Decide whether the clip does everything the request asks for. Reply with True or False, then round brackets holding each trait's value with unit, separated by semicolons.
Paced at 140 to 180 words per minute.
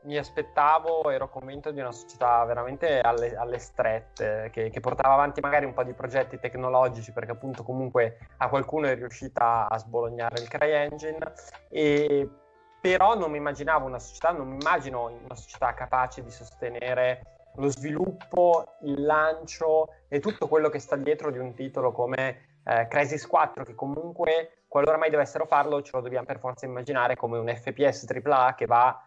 True (170 wpm)